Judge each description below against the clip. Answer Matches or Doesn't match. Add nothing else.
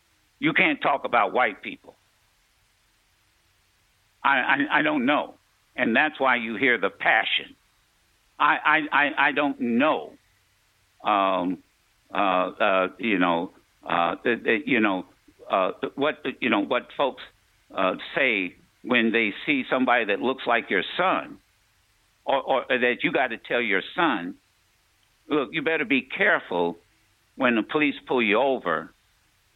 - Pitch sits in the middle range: Doesn't match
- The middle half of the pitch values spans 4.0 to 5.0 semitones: Matches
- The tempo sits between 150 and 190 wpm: Doesn't match